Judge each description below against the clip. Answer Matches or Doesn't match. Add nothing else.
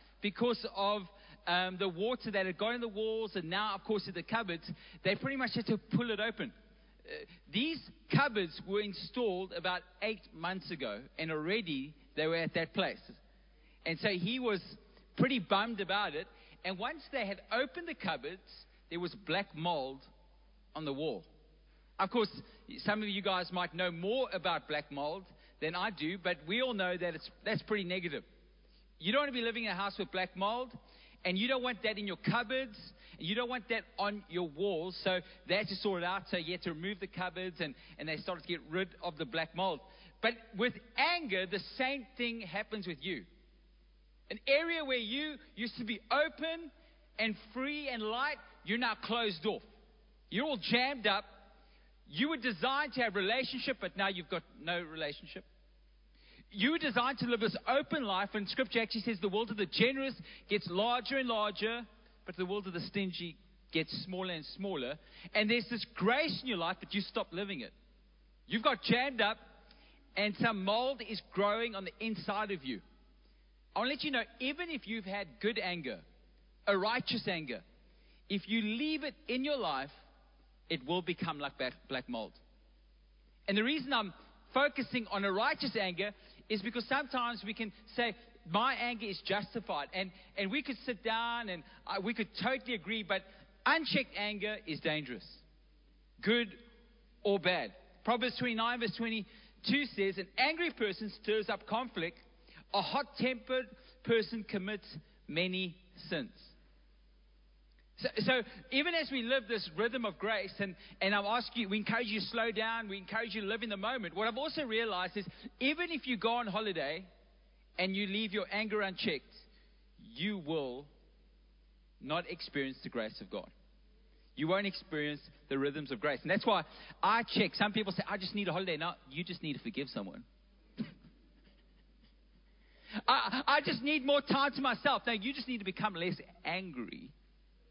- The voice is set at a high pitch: Matches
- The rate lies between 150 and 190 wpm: Matches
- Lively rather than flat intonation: Doesn't match